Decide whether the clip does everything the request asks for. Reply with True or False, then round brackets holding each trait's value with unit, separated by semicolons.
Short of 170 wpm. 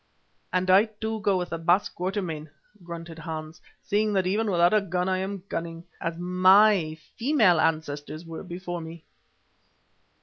True (155 wpm)